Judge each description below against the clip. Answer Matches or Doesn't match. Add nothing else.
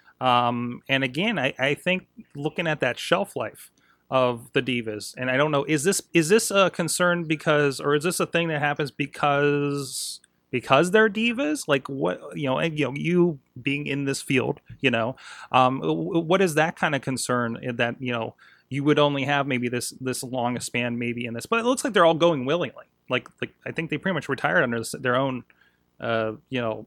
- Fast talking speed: Matches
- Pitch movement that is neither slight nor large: Matches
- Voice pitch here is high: Doesn't match